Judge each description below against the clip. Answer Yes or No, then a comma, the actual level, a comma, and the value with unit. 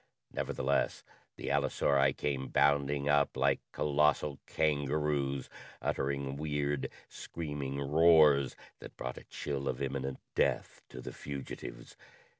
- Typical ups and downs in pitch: No, narrow, 1.2 semitones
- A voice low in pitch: Yes, very low, 70 Hz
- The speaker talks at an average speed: No, slow, 110 wpm